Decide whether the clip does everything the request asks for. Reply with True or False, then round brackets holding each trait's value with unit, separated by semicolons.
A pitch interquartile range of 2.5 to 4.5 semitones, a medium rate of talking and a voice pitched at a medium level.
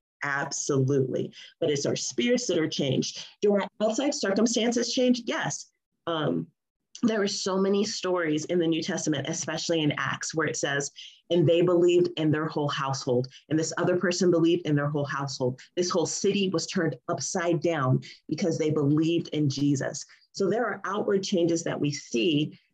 True (3.9 semitones; 175 wpm; 170 Hz)